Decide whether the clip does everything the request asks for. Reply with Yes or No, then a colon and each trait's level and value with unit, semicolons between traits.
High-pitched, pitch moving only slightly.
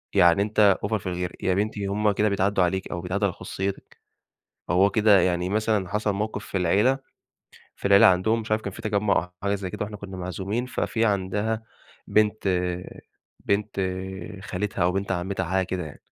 No: low, 100 Hz; narrow, 2.2 semitones